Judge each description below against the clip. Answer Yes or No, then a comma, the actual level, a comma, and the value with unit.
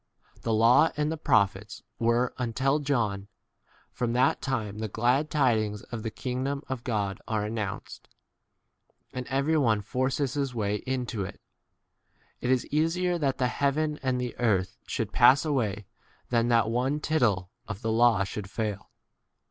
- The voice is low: Yes, low, 120 Hz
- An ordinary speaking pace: Yes, average, 165 wpm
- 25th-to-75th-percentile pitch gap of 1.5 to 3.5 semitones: No, average, 4.1 semitones